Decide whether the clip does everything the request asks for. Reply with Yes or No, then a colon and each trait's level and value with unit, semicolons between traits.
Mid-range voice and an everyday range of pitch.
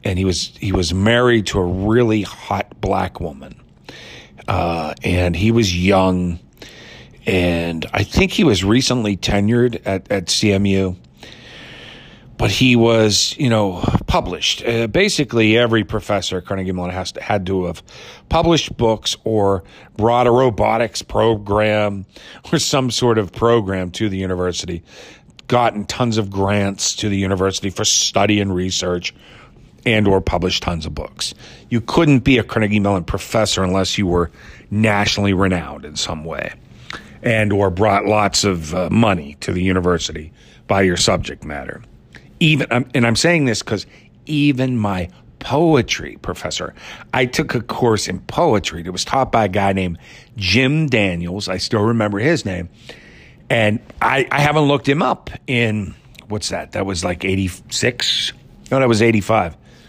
No: low, 105 Hz; average, 4.0 semitones